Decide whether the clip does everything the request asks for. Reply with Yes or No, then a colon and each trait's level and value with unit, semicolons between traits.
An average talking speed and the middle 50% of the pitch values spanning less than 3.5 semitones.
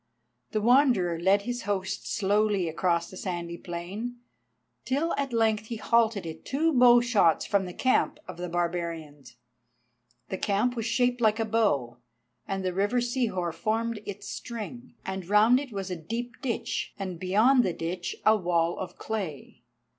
No: average, 160 wpm; average, 5.1 semitones